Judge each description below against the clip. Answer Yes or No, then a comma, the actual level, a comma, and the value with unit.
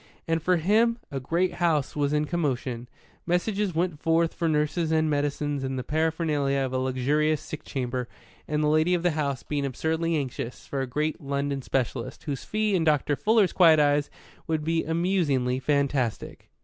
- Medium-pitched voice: Yes, medium, 150 Hz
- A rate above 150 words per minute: Yes, average, 175 wpm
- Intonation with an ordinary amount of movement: Yes, average, 3.2 semitones